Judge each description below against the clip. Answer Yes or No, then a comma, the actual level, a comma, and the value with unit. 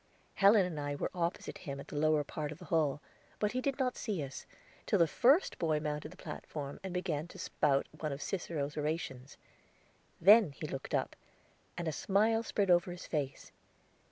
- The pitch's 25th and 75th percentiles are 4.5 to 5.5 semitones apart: Yes, average, 4.8 semitones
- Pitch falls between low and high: Yes, medium, 160 Hz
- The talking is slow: No, average, 190 wpm